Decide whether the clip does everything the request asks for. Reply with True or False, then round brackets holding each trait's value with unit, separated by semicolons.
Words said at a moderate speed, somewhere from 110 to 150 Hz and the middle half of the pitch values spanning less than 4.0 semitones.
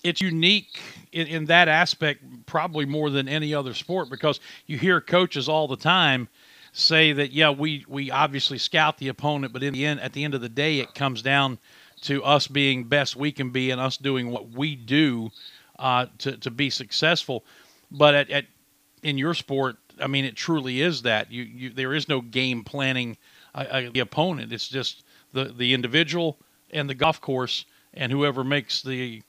True (195 wpm; 140 Hz; 2.9 semitones)